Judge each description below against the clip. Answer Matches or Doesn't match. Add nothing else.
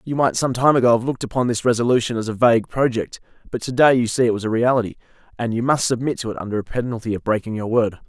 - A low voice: Matches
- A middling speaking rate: Doesn't match